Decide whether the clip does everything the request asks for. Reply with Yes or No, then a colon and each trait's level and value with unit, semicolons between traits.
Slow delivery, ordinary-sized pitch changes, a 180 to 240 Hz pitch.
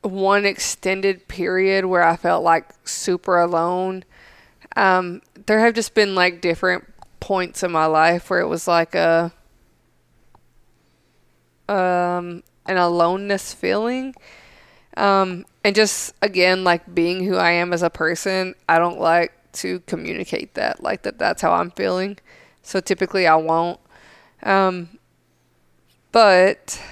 No: slow, 130 wpm; narrow, 2.2 semitones; medium, 185 Hz